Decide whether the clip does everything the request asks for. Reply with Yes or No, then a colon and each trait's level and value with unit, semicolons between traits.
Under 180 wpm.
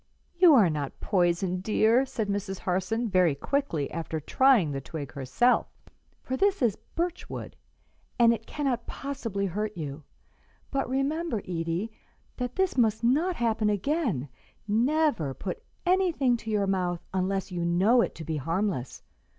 Yes: average, 150 wpm